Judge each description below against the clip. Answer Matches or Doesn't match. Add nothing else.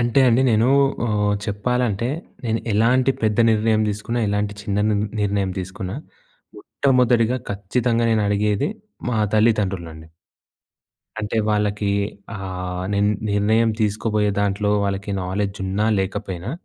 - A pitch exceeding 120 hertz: Doesn't match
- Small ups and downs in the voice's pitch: Matches